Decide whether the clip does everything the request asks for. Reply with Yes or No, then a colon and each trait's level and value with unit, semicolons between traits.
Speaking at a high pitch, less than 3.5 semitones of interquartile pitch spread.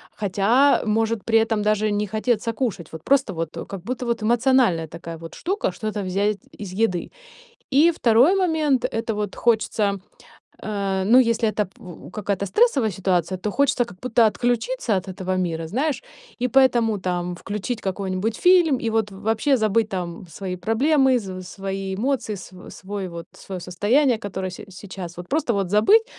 No: high, 210 Hz; average, 4.4 semitones